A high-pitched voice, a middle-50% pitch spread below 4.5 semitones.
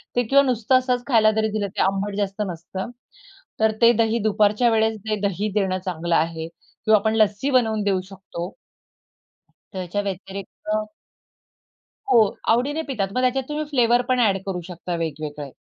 Yes: high, 210 Hz; average, 3.7 semitones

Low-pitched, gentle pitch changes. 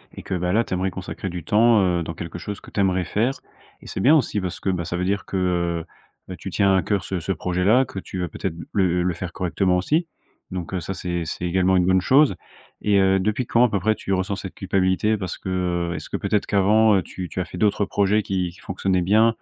Yes: very low, 95 Hz; narrow, 2.3 semitones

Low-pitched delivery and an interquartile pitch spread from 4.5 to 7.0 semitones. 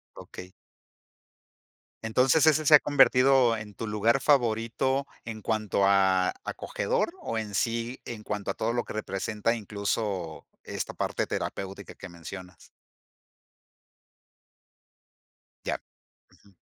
No: low, 110 Hz; average, 3.9 semitones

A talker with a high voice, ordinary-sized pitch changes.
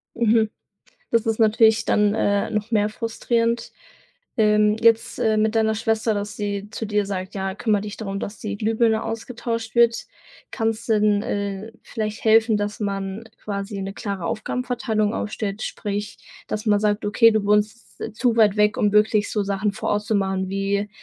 No: high, 215 Hz; narrow, 1.5 semitones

